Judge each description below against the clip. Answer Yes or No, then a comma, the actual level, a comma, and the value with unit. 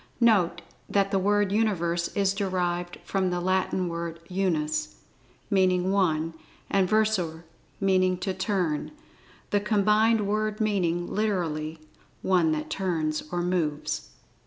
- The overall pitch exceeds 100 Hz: Yes, medium, 185 Hz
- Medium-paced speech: No, slow, 120 wpm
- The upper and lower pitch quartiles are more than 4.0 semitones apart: No, average, 3.0 semitones